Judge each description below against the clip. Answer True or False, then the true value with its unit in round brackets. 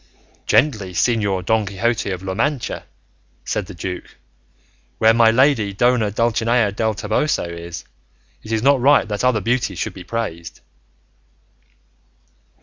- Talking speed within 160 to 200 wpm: False (135 wpm)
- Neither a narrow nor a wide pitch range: True (3.6 semitones)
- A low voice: True (110 Hz)